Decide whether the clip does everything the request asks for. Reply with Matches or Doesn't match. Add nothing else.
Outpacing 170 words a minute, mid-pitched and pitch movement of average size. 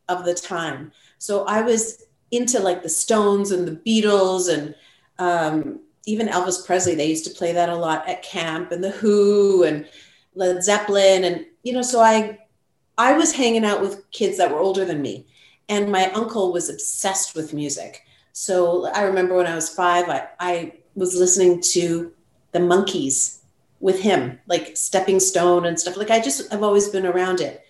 Matches